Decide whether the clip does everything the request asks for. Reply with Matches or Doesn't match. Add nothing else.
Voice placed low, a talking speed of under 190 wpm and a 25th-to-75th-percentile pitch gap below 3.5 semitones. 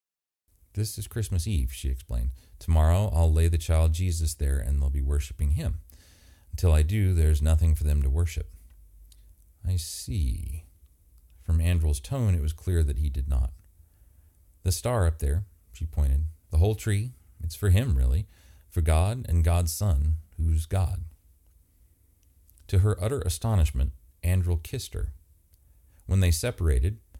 Matches